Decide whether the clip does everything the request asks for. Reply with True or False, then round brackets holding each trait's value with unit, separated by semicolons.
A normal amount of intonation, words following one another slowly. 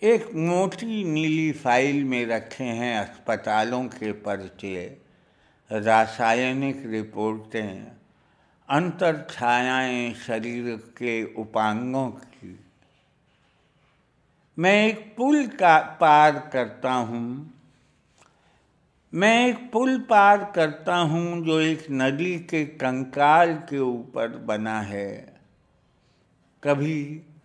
False (6.0 semitones; 90 wpm)